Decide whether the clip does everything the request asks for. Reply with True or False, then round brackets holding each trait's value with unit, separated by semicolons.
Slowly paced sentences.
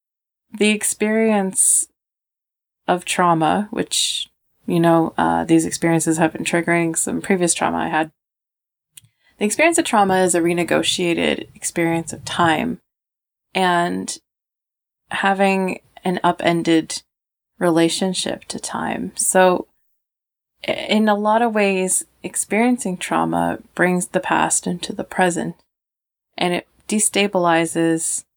True (110 wpm)